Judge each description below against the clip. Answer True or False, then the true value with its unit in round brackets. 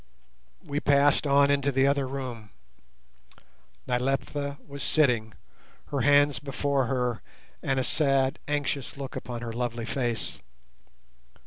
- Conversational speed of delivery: False (120 wpm)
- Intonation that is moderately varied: False (2.3 semitones)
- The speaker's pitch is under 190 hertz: True (135 Hz)